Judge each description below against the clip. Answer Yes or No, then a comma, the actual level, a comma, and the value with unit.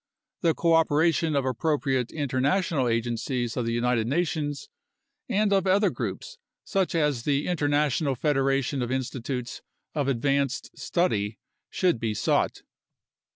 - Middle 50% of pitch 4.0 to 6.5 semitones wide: Yes, average, 4.6 semitones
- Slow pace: Yes, slow, 130 wpm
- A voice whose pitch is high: No, medium, 140 Hz